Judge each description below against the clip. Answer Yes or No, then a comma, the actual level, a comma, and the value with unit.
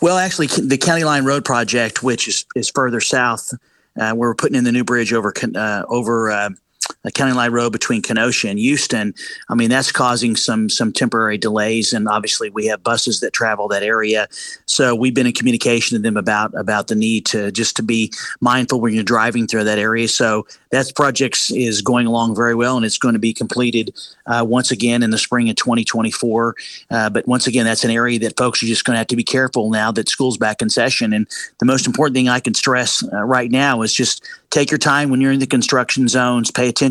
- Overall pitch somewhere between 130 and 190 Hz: No, low, 120 Hz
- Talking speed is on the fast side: Yes, fast, 230 wpm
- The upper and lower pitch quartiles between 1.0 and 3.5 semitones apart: Yes, average, 2.7 semitones